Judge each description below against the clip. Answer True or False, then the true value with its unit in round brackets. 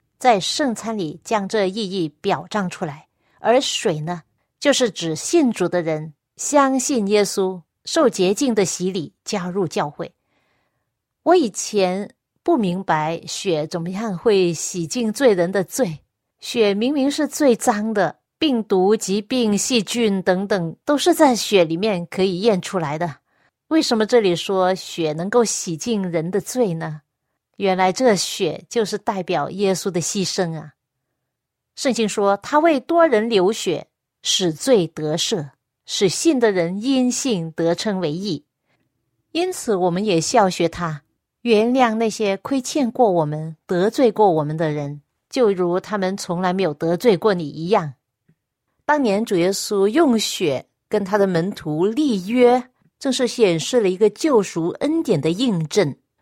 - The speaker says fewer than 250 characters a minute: True (210 characters per minute)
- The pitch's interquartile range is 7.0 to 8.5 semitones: False (5.4 semitones)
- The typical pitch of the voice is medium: False (195 Hz)